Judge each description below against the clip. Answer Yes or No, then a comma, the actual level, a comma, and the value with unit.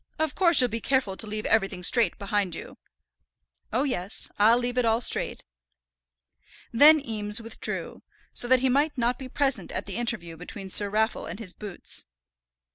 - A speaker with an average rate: Yes, average, 175 wpm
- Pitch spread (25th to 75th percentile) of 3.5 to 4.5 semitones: Yes, average, 3.8 semitones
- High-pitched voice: Yes, high, 230 Hz